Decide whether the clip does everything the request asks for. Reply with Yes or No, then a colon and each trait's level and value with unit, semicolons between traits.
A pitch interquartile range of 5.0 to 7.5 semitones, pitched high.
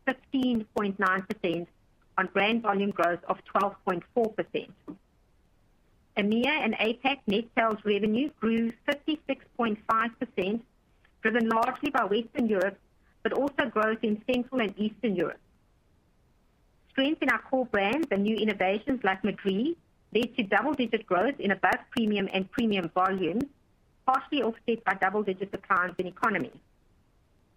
No: average, 4.1 semitones; high, 220 Hz